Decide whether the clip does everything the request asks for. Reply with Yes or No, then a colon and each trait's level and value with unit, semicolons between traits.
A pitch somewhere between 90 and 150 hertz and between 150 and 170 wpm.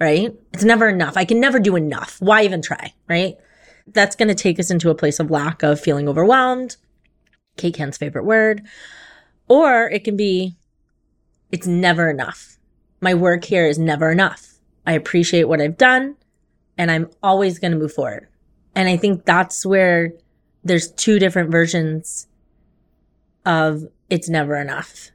No: medium, 175 Hz; average, 160 wpm